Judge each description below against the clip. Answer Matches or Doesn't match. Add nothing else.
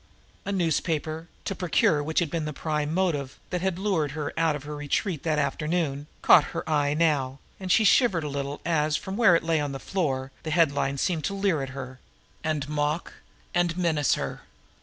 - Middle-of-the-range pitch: Matches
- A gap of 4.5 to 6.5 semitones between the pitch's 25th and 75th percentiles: Doesn't match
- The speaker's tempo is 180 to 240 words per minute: Matches